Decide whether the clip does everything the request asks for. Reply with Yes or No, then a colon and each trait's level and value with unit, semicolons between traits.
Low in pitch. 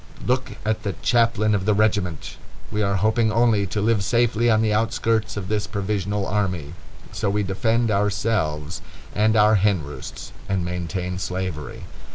Yes: low, 105 Hz